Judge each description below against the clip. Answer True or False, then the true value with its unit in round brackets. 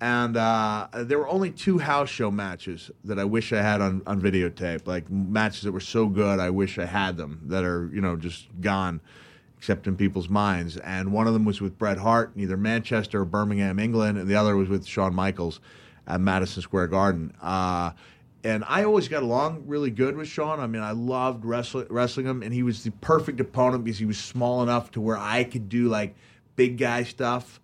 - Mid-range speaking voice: False (105 Hz)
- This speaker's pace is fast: True (215 wpm)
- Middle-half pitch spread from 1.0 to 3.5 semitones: False (4.0 semitones)